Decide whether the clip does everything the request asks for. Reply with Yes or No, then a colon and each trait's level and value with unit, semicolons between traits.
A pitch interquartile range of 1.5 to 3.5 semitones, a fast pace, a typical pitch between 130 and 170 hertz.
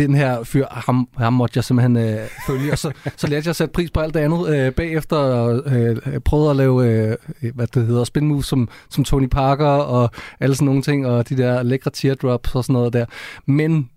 Yes: average, 2.9 semitones; fast, 230 wpm; low, 135 Hz